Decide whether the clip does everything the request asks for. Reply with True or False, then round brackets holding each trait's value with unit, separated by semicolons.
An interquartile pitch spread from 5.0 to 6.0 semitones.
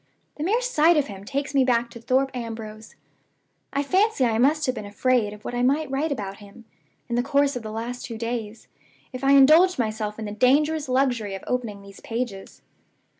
False (4.3 semitones)